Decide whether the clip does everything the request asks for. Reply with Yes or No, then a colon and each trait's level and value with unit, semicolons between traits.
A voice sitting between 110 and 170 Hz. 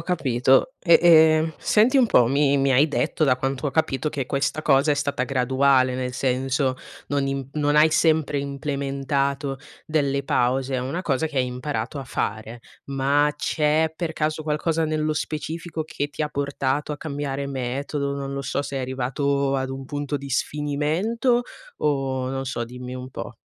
Yes: medium, 140 Hz